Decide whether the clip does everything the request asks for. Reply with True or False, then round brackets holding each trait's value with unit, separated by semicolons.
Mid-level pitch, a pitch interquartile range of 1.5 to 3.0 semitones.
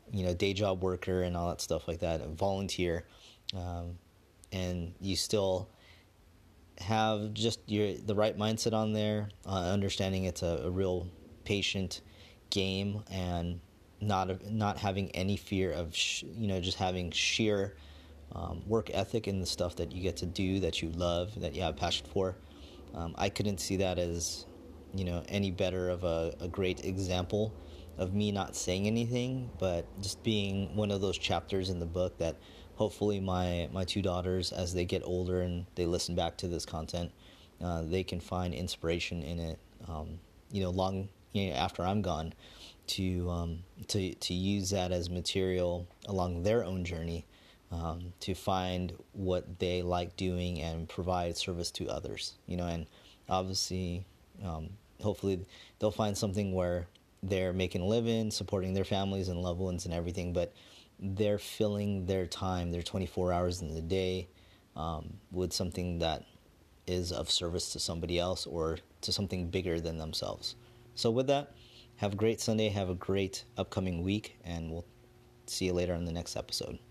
False (90 Hz; 2.4 semitones)